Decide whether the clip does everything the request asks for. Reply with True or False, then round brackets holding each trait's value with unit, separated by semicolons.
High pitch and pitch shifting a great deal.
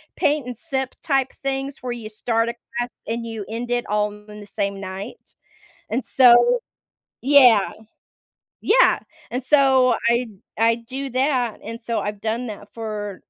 False (235 Hz; 3.5 semitones)